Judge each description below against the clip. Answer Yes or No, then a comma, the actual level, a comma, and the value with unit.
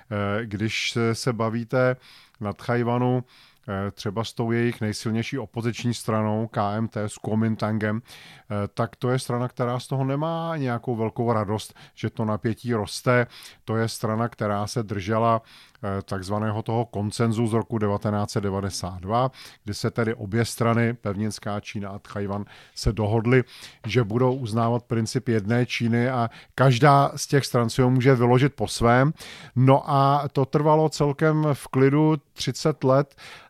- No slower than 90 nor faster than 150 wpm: Yes, average, 140 wpm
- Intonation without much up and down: No, average, 3.2 semitones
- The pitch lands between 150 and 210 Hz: No, low, 115 Hz